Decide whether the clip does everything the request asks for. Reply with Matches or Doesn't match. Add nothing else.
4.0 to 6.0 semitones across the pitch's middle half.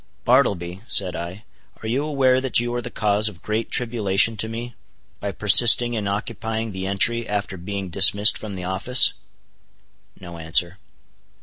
Doesn't match